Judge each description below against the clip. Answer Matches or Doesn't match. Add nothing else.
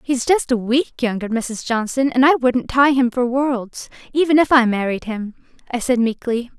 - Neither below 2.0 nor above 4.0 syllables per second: Doesn't match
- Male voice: Doesn't match